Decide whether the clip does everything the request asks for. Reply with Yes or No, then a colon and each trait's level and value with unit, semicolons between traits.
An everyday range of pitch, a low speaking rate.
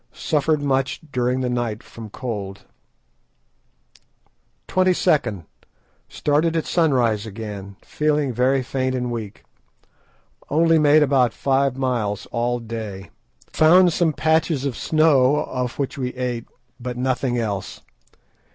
Yes: average, 4.1 semitones; slow, 115 wpm